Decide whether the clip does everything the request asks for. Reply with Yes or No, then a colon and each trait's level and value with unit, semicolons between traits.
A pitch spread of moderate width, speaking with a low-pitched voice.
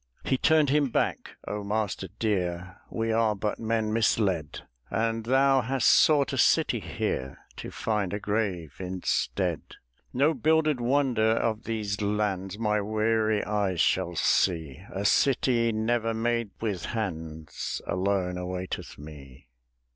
Yes: average, 3.8 semitones; low, 105 Hz